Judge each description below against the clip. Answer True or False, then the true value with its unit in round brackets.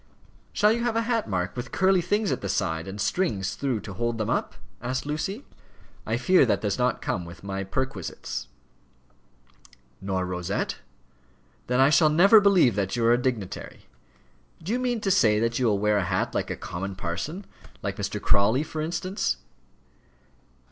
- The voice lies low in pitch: True (120 Hz)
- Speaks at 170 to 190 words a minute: True (180 wpm)